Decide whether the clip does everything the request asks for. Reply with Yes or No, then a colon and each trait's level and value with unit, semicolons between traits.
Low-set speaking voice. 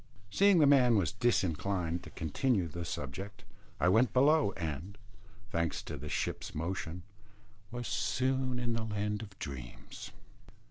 Yes: low, 100 Hz